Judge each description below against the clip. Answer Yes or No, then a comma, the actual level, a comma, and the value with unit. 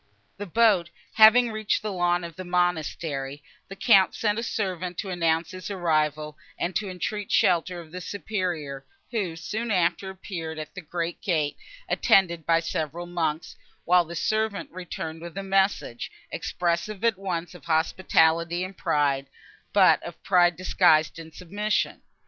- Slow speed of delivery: No, average, 155 wpm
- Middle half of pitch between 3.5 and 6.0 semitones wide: No, average, 3.0 semitones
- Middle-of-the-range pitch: Yes, medium, 175 Hz